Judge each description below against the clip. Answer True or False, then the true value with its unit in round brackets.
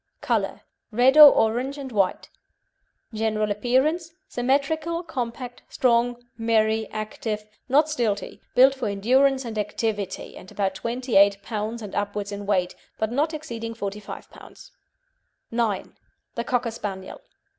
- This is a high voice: True (230 Hz)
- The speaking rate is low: True (125 wpm)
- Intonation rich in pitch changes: False (3.9 semitones)